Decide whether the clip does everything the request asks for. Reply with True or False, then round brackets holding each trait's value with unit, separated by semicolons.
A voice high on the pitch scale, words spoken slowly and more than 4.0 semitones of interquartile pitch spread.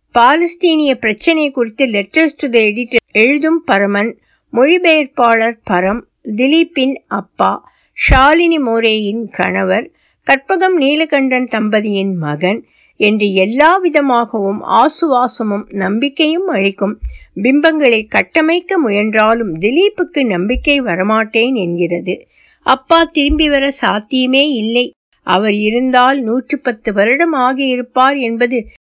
False (250 Hz; 90 wpm; 5.4 semitones)